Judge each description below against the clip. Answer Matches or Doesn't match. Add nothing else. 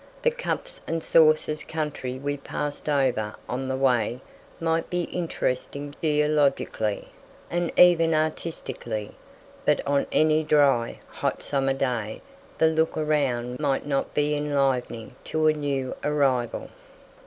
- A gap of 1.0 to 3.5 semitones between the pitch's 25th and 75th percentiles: Matches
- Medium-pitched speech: Matches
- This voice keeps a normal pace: Doesn't match